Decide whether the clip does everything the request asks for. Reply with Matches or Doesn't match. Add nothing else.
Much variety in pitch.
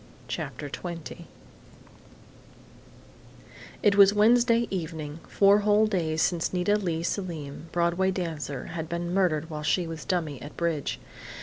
Doesn't match